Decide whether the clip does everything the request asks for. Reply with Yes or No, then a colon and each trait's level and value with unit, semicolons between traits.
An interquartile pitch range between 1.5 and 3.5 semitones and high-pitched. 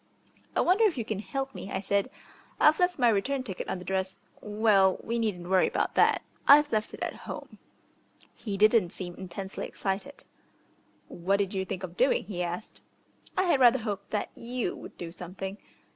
No: average, 4.4 semitones; high, 205 Hz